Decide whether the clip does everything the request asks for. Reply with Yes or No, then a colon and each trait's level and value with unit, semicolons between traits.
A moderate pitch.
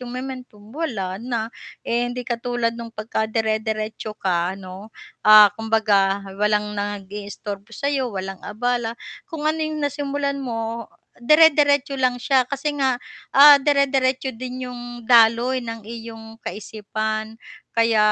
No: high, 230 Hz